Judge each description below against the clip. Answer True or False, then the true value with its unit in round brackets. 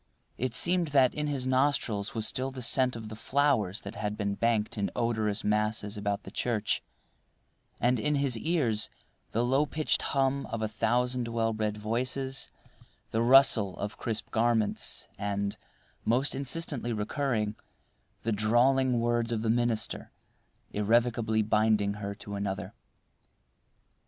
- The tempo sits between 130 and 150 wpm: True (140 wpm)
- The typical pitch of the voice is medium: False (115 Hz)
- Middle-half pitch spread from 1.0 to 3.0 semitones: False (3.4 semitones)